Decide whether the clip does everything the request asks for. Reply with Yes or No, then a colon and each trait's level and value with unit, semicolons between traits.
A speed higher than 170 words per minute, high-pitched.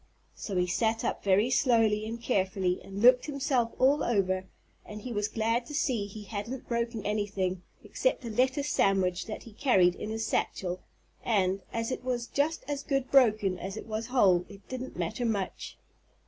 Yes: average, 185 wpm; high, 220 Hz